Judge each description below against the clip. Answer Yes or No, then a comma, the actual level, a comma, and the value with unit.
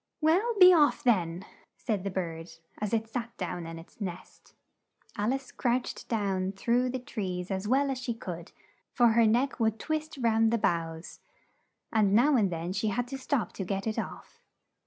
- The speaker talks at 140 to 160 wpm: No, average, 185 wpm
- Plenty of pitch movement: No, average, 5.0 semitones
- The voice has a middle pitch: No, high, 220 Hz